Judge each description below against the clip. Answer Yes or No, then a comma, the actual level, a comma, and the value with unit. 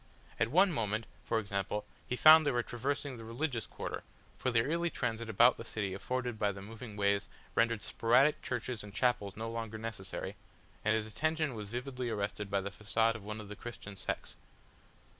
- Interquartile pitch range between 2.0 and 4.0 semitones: Yes, average, 3.1 semitones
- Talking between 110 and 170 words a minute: No, average, 190 wpm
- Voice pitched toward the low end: Yes, low, 115 Hz